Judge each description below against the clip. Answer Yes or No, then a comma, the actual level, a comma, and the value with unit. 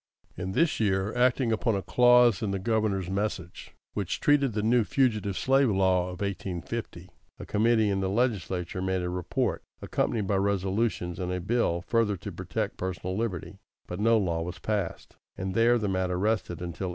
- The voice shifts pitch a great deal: No, average, 3.7 semitones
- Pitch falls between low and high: No, low, 100 Hz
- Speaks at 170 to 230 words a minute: Yes, average, 185 wpm